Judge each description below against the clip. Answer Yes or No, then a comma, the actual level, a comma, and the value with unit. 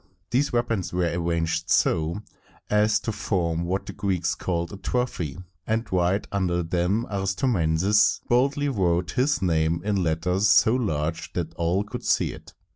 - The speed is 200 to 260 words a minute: No, average, 150 wpm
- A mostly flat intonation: No, average, 4.1 semitones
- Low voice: Yes, very low, 95 Hz